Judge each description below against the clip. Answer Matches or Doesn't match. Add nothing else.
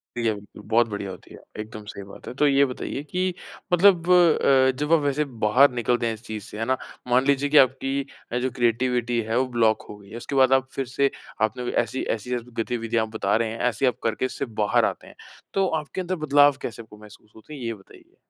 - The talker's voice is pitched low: Matches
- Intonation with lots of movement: Doesn't match